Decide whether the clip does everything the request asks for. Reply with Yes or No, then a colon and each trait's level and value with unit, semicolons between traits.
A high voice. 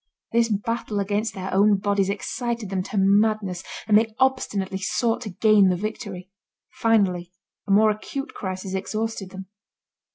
Yes: high, 205 Hz